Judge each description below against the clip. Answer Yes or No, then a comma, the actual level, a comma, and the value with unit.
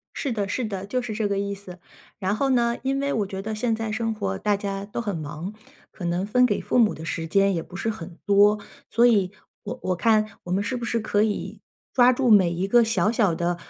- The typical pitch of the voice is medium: No, high, 205 Hz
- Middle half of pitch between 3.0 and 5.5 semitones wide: Yes, average, 3.3 semitones